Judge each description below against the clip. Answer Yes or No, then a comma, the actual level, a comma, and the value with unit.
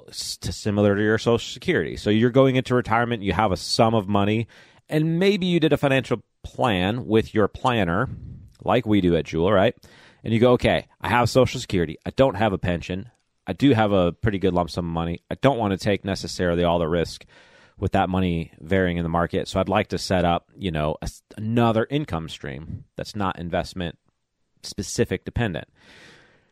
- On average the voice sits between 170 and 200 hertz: No, low, 100 Hz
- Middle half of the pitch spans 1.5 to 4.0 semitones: No, average, 4.6 semitones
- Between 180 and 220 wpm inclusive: Yes, average, 195 wpm